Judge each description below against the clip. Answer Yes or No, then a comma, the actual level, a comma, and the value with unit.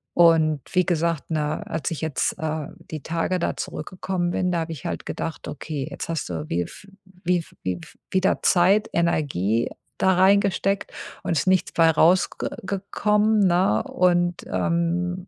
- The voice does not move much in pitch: No, average, 3.0 semitones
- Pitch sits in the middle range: Yes, medium, 170 Hz